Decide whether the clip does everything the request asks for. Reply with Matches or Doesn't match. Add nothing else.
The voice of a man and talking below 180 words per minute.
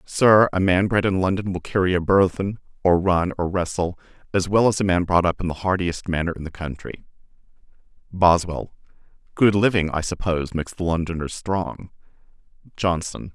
Matches